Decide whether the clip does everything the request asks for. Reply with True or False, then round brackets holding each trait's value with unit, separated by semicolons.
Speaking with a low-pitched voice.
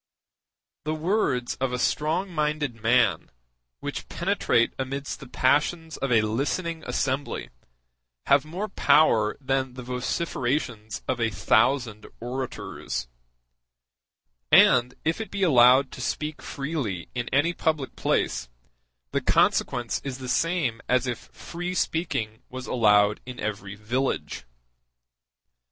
True (130 Hz)